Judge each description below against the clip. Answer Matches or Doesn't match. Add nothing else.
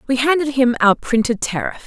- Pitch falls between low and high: Doesn't match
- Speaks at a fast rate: Doesn't match